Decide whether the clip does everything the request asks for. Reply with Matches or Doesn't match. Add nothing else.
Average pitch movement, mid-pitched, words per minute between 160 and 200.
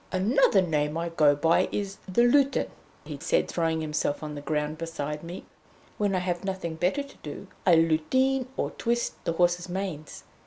Matches